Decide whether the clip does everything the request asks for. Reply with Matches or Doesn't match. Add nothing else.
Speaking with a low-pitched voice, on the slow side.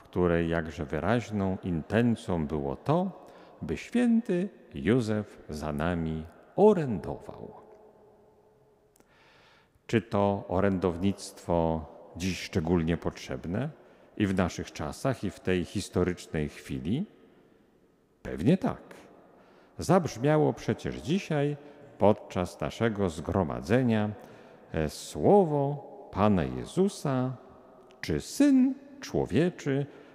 Matches